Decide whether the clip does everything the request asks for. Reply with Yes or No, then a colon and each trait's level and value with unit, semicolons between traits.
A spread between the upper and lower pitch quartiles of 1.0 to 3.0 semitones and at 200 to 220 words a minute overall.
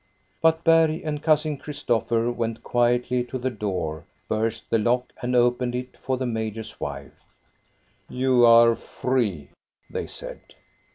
No: narrow, 2.4 semitones; average, 145 wpm